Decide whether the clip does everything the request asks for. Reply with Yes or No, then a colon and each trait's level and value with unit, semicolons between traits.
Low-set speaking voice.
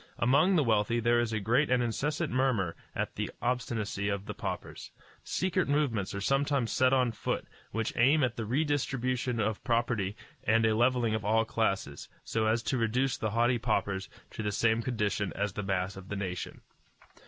Yes: low, 115 Hz